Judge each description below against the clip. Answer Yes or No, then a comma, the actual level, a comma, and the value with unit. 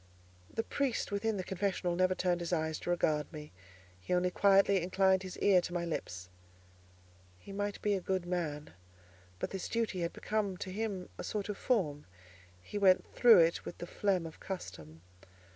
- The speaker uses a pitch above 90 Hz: Yes, medium, 185 Hz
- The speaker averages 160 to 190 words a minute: Yes, average, 180 wpm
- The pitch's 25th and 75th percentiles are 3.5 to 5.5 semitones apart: No, average, 2.8 semitones